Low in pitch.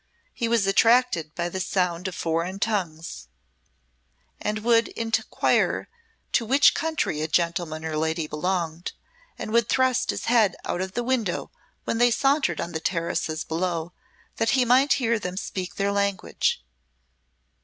No: high, 190 Hz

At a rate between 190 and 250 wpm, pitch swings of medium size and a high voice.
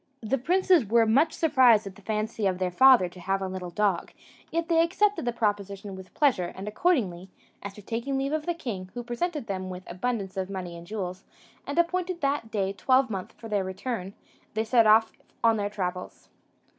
No: average, 195 wpm; wide, 6.0 semitones; high, 215 Hz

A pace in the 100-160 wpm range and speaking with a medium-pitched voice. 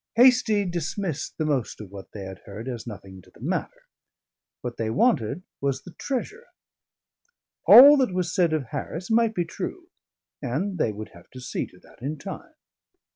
No: average, 180 wpm; medium, 160 Hz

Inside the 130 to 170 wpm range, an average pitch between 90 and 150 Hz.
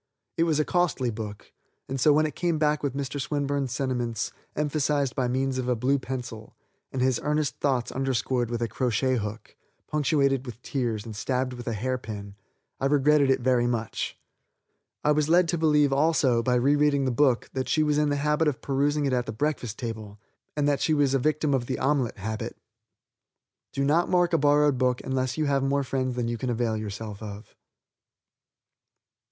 No: average, 195 wpm; low, 135 Hz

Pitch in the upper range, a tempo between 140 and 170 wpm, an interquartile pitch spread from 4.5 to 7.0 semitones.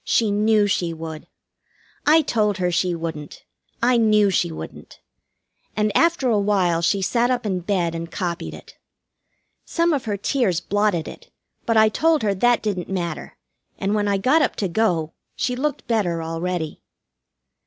Yes: high, 205 Hz; average, 165 wpm; average, 4.8 semitones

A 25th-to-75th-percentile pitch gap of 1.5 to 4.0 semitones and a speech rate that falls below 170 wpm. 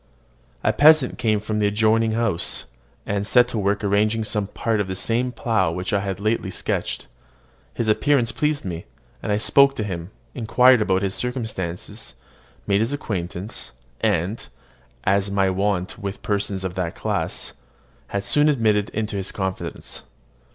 Yes: average, 2.9 semitones; average, 160 wpm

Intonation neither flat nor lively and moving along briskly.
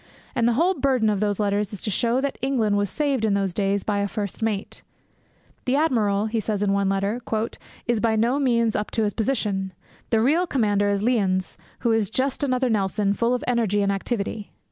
Yes: average, 3.5 semitones; fast, 210 wpm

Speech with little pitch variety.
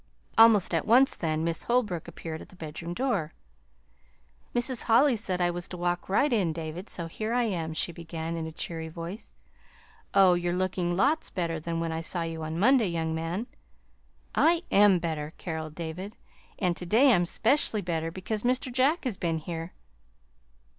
No: average, 5.0 semitones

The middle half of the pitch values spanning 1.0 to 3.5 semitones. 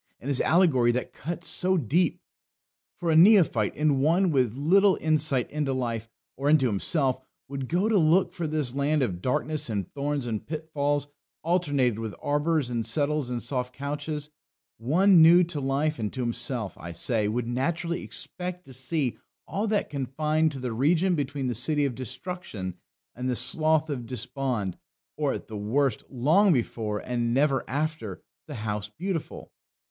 No: average, 4.4 semitones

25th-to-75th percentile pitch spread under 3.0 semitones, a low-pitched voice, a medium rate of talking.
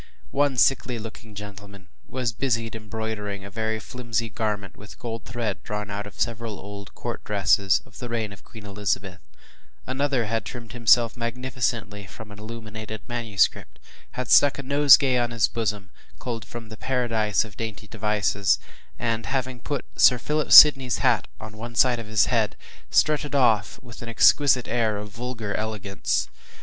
Yes: narrow, 2.6 semitones; low, 110 Hz; average, 160 wpm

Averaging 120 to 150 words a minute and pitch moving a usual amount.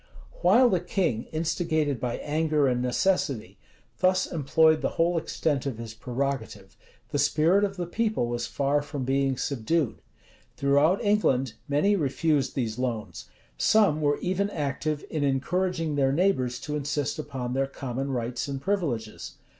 Yes: average, 145 wpm; average, 4.4 semitones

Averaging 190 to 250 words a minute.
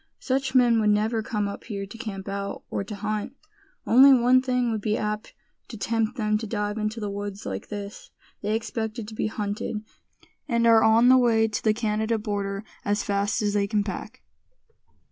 Yes: average, 195 wpm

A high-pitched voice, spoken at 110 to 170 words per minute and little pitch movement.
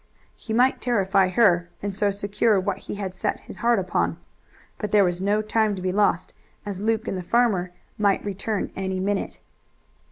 No: high, 200 Hz; average, 185 wpm; narrow, 2.2 semitones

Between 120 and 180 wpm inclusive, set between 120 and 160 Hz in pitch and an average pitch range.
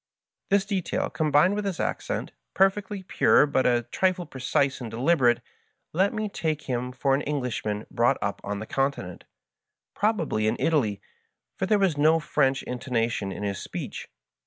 No: average, 165 wpm; medium, 140 Hz; wide, 7.4 semitones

